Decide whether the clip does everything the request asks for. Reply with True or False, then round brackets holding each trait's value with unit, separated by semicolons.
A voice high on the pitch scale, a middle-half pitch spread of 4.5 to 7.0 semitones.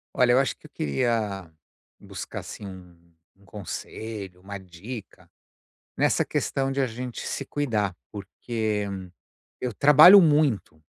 False (110 Hz; 5.0 semitones)